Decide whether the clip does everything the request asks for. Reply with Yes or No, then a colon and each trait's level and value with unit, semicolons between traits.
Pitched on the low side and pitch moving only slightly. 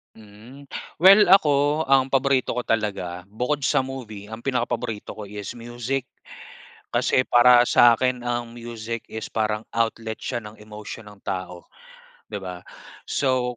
No: low, 115 Hz; average, 3.3 semitones